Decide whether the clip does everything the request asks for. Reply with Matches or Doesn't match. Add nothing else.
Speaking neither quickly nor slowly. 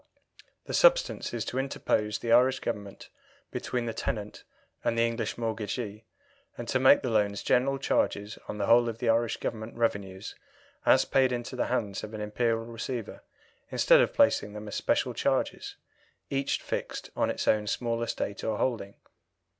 Matches